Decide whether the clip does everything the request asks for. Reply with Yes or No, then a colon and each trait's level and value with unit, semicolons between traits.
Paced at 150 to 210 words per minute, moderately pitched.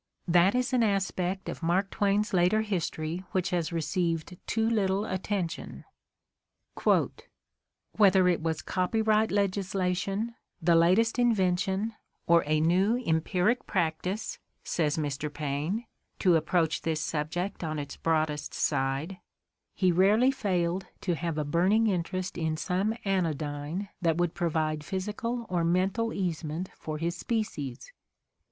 No: slow, 135 wpm; medium, 180 Hz